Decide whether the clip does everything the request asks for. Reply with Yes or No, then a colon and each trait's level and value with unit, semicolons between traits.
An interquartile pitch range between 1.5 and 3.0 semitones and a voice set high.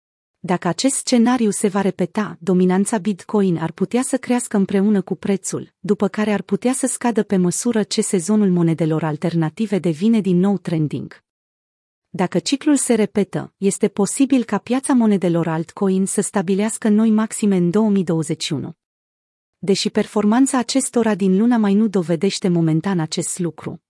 No: average, 3.8 semitones; high, 200 Hz